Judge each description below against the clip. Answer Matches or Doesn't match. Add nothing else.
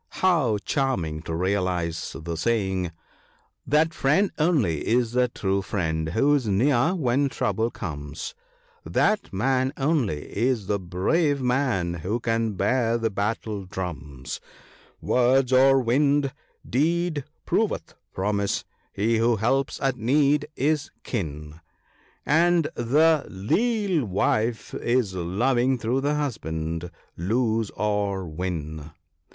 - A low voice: Matches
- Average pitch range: Doesn't match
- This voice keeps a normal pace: Doesn't match